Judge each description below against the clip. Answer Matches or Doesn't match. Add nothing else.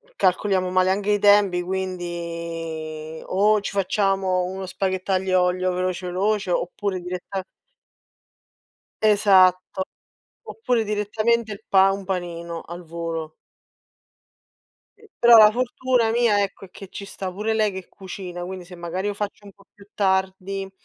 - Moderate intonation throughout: Doesn't match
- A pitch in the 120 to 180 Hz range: Doesn't match